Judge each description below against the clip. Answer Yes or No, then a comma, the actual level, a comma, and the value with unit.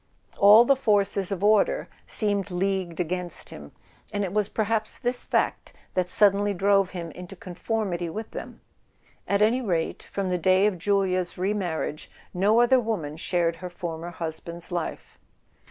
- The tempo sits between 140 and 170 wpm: Yes, average, 155 wpm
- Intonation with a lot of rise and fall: No, average, 3.0 semitones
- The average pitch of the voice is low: No, high, 190 Hz